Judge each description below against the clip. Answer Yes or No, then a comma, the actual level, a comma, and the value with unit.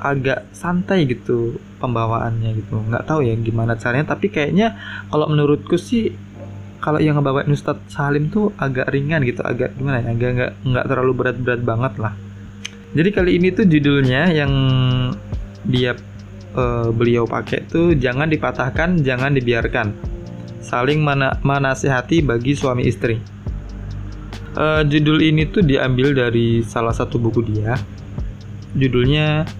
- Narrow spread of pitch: No, average, 4.5 semitones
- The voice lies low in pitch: Yes, low, 125 Hz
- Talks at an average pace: Yes, average, 130 wpm